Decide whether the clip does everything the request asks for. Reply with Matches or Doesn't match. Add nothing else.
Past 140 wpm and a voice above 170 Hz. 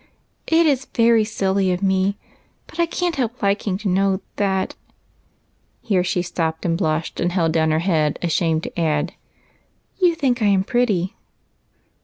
Matches